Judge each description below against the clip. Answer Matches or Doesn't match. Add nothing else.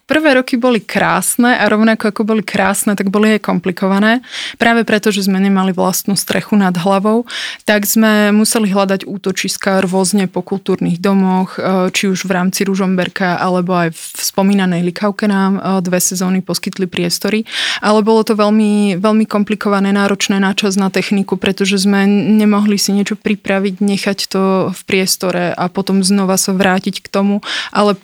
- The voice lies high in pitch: Matches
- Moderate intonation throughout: Doesn't match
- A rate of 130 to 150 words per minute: Doesn't match